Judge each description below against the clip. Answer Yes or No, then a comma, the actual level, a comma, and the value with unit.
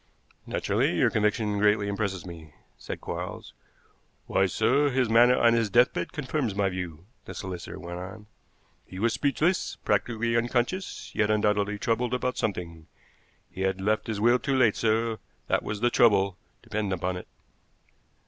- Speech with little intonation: No, average, 3.8 semitones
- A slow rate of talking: No, average, 155 wpm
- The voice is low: Yes, low, 105 Hz